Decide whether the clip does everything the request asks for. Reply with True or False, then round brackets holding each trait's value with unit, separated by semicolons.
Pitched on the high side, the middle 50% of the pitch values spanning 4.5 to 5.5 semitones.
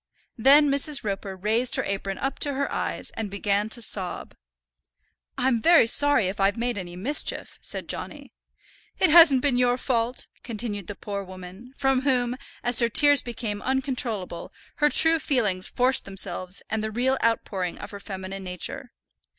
True (230 Hz; 5.1 semitones)